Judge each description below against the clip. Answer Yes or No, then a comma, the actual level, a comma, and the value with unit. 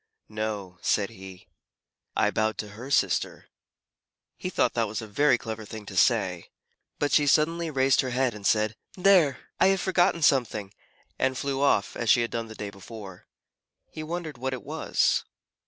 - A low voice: Yes, low, 115 Hz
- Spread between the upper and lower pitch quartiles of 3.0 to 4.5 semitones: No, average, 5.1 semitones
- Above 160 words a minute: Yes, average, 175 wpm